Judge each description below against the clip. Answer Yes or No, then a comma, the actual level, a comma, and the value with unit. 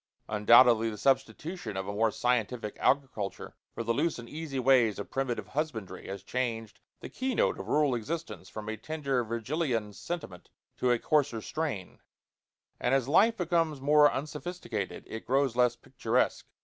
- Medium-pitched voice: No, low, 125 Hz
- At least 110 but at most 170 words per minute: Yes, average, 160 wpm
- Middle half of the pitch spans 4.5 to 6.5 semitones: Yes, average, 5.2 semitones